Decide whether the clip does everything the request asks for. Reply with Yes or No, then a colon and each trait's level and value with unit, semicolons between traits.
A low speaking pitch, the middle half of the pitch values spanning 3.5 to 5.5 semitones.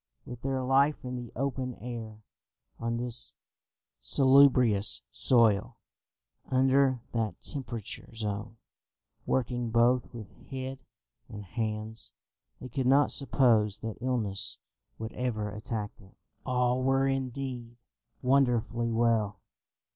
No: low, 120 Hz; average, 2.8 semitones